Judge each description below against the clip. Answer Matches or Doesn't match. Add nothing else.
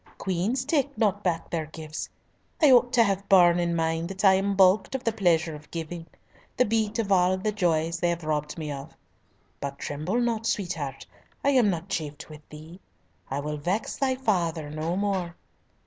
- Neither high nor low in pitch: Matches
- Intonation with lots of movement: Doesn't match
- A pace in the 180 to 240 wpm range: Matches